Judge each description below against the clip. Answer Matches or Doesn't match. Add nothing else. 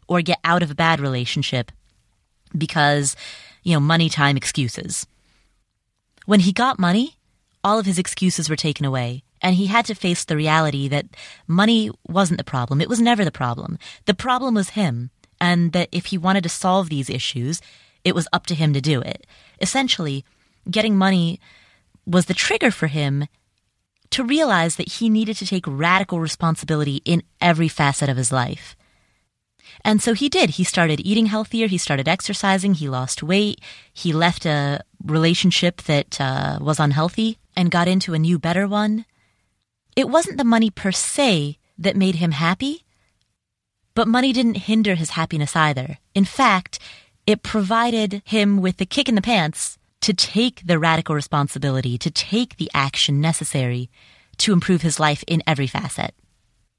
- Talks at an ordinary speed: Matches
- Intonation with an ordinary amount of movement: Doesn't match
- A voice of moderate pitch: Matches